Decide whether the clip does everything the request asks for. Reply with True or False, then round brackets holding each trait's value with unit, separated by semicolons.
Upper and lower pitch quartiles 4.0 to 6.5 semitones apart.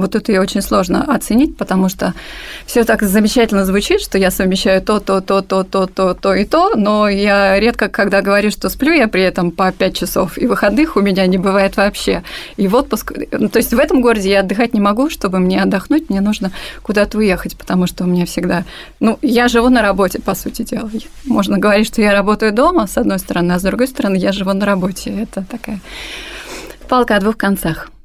False (3.0 semitones)